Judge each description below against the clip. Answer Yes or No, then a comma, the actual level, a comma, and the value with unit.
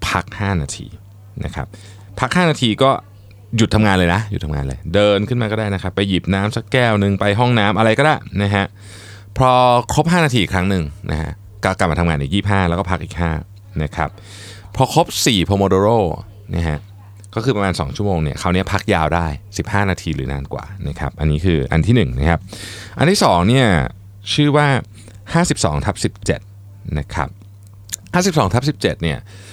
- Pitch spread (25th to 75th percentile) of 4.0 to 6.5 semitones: No, average, 3.5 semitones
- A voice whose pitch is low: Yes, low, 100 Hz